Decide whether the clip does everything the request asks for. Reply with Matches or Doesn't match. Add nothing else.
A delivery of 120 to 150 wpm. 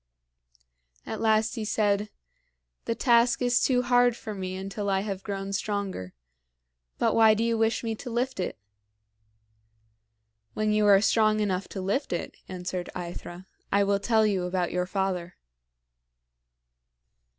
Matches